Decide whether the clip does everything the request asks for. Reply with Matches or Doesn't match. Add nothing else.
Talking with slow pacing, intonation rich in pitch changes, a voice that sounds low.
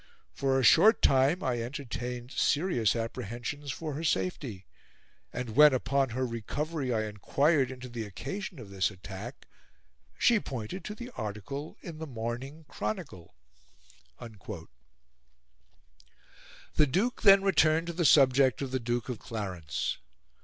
Matches